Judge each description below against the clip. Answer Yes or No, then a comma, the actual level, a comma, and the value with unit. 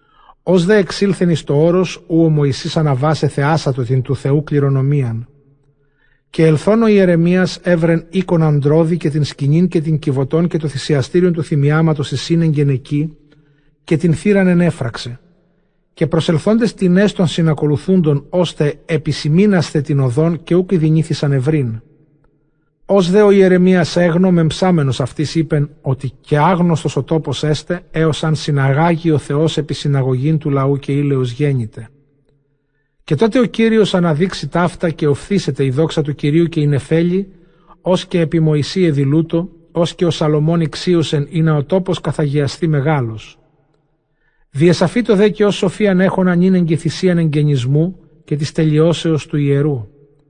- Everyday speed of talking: Yes, average, 150 wpm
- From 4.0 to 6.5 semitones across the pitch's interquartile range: No, average, 3.3 semitones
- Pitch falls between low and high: Yes, medium, 155 Hz